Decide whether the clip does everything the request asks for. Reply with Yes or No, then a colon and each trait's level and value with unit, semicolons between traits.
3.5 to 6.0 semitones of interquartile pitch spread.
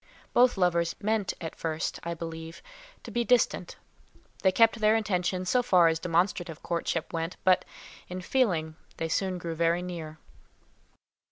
No: average, 3.1 semitones